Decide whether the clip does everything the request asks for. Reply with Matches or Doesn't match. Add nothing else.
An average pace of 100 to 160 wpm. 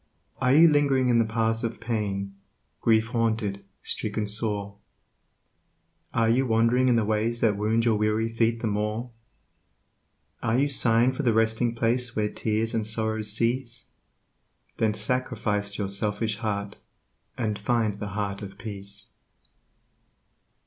Matches